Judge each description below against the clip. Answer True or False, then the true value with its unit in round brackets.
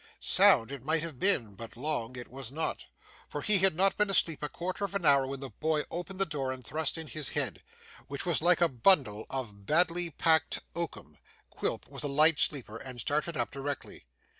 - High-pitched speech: False (150 Hz)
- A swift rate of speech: True (210 wpm)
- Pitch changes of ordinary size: True (4.5 semitones)